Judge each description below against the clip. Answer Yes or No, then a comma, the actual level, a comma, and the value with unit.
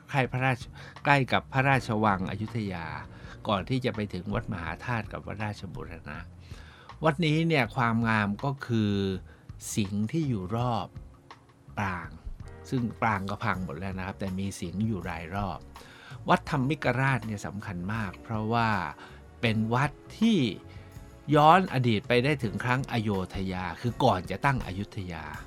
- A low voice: Yes, low, 105 Hz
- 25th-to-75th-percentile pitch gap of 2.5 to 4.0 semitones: No, average, 4.6 semitones